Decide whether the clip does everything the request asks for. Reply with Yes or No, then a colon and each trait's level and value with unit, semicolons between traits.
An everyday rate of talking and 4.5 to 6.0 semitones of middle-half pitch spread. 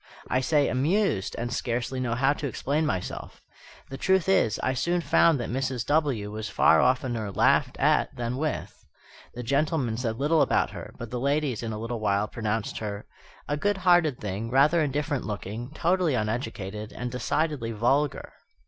Yes: average, 170 wpm; average, 4.8 semitones